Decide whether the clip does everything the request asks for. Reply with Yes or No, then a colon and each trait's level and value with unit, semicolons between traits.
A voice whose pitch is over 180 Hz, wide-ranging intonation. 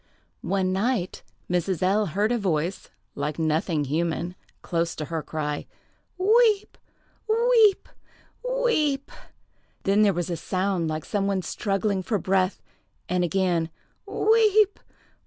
Yes: high, 190 Hz; wide, 5.9 semitones